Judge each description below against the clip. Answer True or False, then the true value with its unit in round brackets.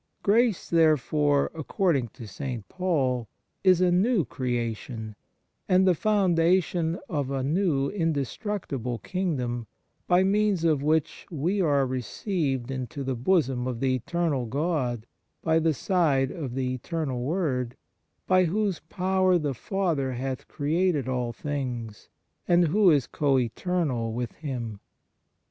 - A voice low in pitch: False (145 Hz)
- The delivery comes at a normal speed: False (130 wpm)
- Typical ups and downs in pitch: False (5.9 semitones)